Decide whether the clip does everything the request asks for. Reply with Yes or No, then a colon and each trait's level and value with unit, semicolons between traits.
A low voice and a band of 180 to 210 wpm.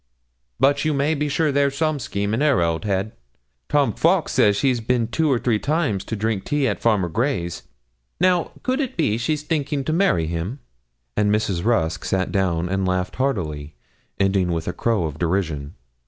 Yes: low, 110 Hz; average, 185 wpm